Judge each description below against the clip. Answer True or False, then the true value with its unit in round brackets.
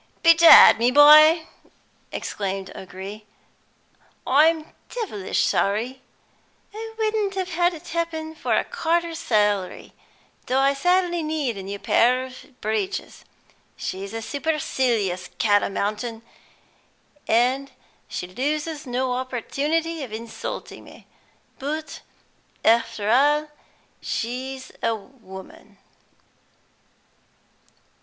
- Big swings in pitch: True (6.5 semitones)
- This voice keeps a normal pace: False (100 wpm)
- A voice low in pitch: False (260 Hz)